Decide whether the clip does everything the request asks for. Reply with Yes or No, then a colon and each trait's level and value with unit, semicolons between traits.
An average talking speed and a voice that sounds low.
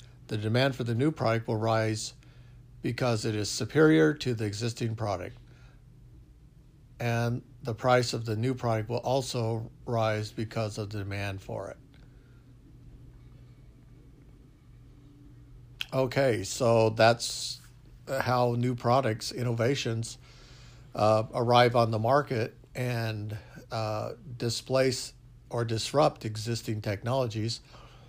No: slow, 110 wpm; low, 125 Hz